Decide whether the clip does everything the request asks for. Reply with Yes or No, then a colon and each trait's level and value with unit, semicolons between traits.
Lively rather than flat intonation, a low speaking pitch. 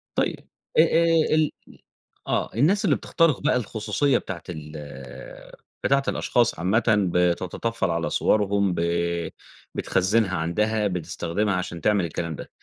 Yes: wide, 5.8 semitones; low, 100 Hz